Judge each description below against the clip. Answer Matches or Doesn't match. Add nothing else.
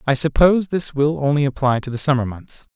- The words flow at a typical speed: Doesn't match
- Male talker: Matches